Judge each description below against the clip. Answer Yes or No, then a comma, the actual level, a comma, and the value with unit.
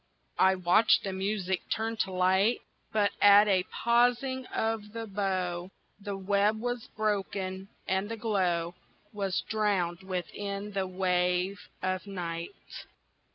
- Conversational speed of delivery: No, slow, 125 wpm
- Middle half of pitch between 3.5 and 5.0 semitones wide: No, narrow, 2.5 semitones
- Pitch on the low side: No, high, 195 Hz